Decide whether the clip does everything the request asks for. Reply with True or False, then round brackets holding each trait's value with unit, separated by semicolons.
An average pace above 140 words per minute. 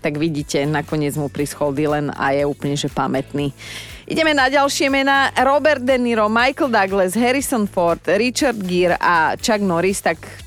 True (160 wpm)